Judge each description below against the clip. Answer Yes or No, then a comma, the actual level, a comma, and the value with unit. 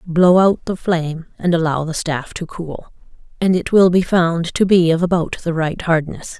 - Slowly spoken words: No, fast, 205 wpm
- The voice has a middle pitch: Yes, medium, 170 Hz